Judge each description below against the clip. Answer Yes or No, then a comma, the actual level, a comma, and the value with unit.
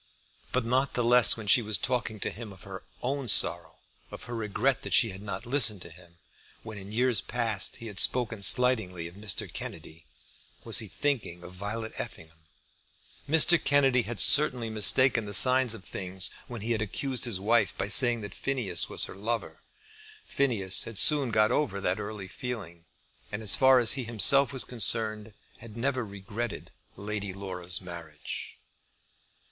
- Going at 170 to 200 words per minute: Yes, average, 175 wpm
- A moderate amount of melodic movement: Yes, average, 4.2 semitones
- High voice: No, low, 110 Hz